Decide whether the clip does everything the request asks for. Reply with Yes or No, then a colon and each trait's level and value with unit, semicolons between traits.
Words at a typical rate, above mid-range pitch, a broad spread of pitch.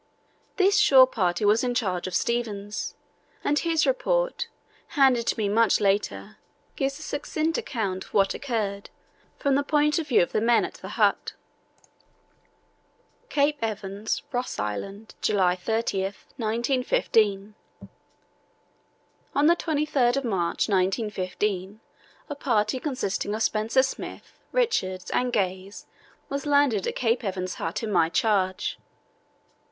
No: slow, 130 wpm; high, 225 Hz; wide, 5.9 semitones